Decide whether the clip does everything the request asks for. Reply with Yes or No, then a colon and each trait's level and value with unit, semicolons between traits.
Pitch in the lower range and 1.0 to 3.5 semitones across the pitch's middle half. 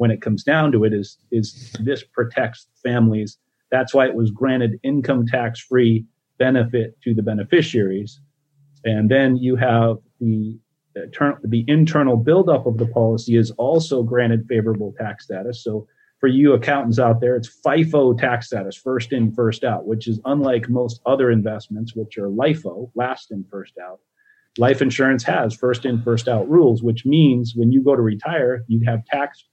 Yes: low, 120 Hz; average, 2.9 semitones